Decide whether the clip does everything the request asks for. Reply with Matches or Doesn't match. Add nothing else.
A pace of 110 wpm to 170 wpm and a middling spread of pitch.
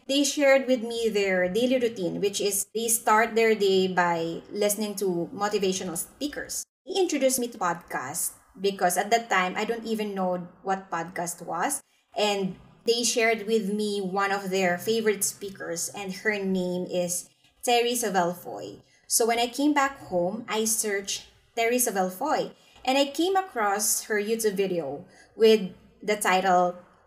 Matches